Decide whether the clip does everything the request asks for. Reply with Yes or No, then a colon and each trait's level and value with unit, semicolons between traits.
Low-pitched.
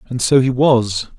Yes: low, 125 Hz